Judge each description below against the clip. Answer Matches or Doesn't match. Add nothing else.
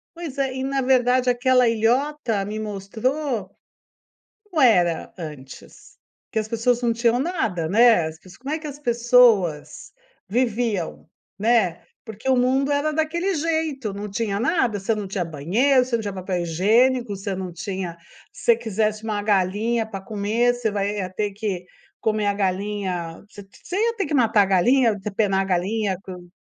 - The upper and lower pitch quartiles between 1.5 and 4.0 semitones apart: Doesn't match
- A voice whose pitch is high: Matches